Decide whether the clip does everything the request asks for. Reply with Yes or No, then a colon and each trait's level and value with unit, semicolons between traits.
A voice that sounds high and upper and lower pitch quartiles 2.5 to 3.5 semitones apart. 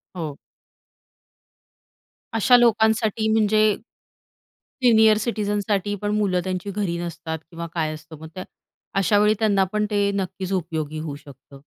No: high, 200 Hz; average, 4.2 semitones